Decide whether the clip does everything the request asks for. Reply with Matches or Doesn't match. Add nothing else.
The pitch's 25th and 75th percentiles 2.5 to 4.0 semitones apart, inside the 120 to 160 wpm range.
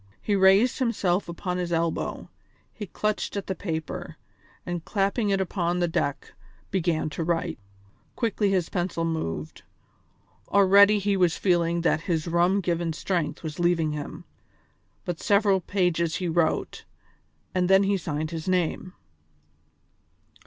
Matches